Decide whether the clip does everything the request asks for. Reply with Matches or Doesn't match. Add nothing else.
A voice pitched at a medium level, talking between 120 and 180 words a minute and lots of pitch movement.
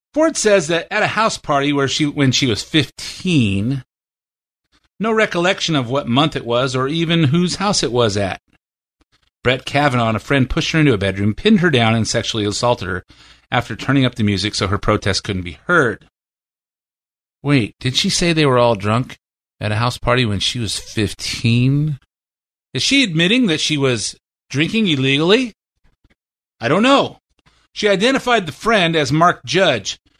Doesn't match